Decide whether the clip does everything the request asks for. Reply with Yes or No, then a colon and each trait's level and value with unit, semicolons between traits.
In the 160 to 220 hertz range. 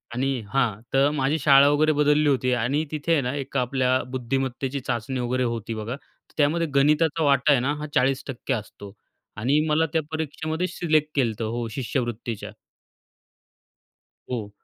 No: low, 135 Hz